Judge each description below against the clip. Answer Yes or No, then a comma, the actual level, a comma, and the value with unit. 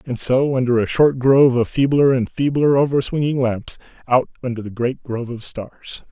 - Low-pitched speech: Yes, low, 130 Hz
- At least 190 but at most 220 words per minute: Yes, average, 195 wpm